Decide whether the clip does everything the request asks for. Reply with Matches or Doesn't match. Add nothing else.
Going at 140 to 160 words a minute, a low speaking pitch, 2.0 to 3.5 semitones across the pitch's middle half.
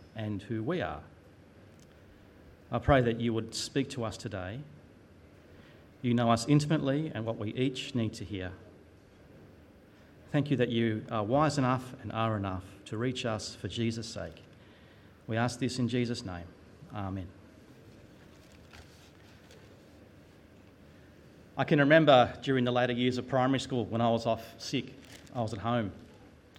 Doesn't match